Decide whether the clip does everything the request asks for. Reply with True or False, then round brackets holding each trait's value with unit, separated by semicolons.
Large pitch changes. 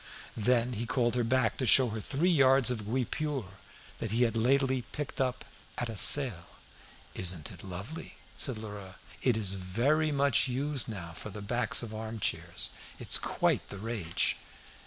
False (4.2 semitones)